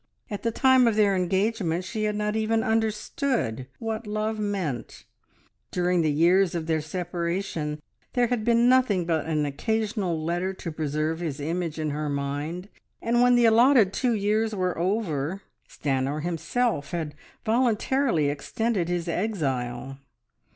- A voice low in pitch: No, medium, 185 Hz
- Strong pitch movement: Yes, wide, 5.8 semitones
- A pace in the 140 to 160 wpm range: Yes, average, 145 wpm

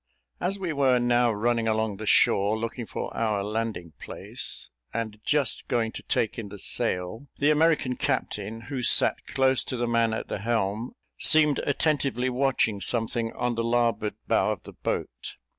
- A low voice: Yes, low, 115 Hz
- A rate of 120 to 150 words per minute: No, average, 170 wpm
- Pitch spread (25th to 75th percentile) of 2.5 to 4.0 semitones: Yes, average, 3.1 semitones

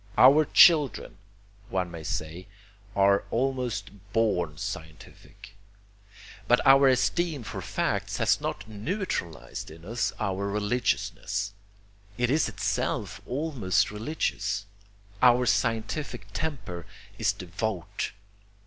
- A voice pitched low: Yes, low, 110 Hz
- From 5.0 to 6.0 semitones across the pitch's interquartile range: Yes, wide, 5.5 semitones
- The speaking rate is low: Yes, slow, 100 wpm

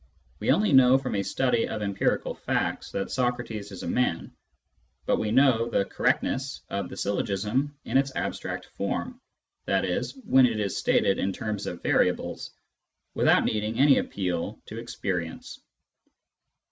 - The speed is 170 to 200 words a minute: No, average, 150 wpm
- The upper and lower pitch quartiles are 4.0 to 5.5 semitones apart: Yes, average, 4.9 semitones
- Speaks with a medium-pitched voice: No, low, 110 Hz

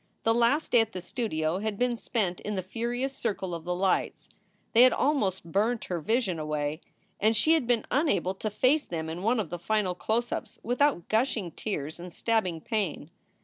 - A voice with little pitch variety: No, average, 5.3 semitones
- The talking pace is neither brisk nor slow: Yes, average, 195 wpm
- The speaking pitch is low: No, high, 210 Hz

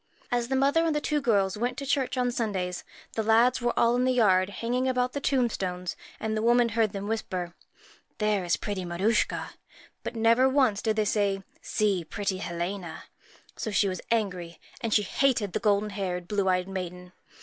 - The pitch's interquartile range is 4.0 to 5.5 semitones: Yes, average, 4.4 semitones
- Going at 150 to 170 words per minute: No, average, 195 wpm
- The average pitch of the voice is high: Yes, high, 215 Hz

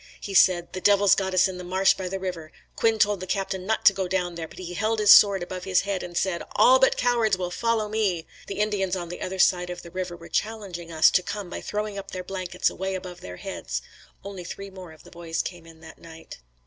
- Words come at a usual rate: No, fast, 250 wpm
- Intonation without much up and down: Yes, narrow, 2.3 semitones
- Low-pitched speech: No, medium, 185 Hz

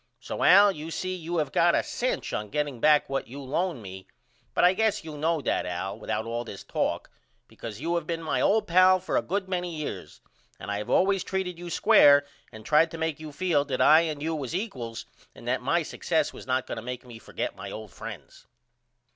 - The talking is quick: Yes, fast, 225 wpm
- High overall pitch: No, medium, 155 Hz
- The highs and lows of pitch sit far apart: Yes, wide, 5.9 semitones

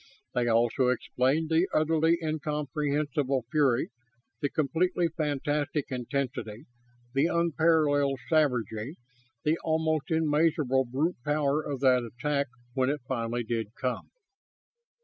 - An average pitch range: Yes, average, 3.6 semitones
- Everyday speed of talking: No, slow, 110 wpm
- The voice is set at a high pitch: No, medium, 145 Hz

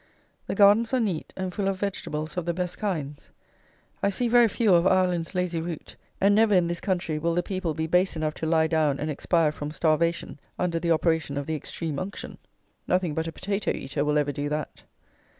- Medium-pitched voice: Yes, medium, 170 Hz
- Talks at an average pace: No, fast, 210 wpm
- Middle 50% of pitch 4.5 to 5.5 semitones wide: No, average, 3.2 semitones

